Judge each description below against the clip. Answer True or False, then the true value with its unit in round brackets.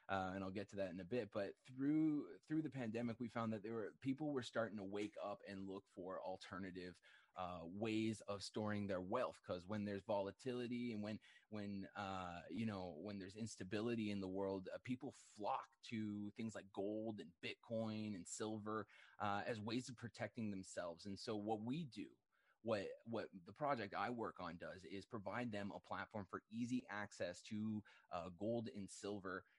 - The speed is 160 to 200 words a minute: True (190 wpm)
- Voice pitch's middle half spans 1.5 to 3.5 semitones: True (3.1 semitones)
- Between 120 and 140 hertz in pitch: False (105 Hz)